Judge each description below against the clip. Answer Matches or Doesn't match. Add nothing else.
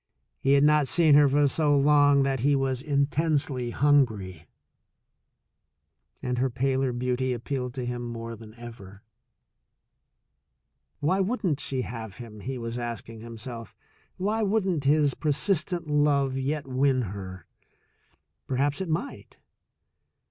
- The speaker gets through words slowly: Matches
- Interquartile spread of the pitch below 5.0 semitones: Matches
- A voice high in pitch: Doesn't match